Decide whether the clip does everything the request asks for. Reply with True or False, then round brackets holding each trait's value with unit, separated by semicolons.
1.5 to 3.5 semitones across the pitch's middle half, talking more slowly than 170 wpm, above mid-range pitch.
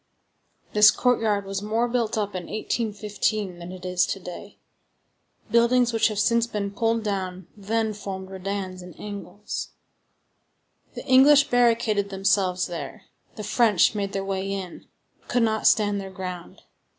True (2.9 semitones; 150 wpm; 205 Hz)